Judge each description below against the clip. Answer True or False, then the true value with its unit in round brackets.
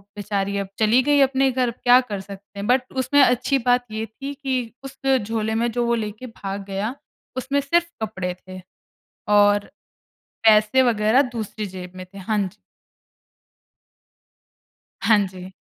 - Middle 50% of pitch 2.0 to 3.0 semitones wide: False (4.2 semitones)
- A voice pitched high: True (220 Hz)